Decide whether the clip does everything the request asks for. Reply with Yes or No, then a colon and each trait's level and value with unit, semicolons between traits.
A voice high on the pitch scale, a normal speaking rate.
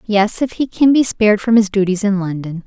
No: high, 205 Hz; fast, 225 wpm